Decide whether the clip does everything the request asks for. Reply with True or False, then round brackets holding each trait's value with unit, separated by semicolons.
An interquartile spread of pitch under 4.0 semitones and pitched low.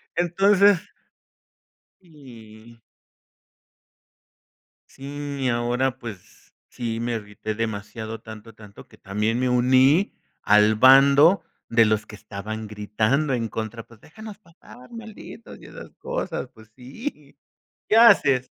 False (4.7 semitones; 120 Hz)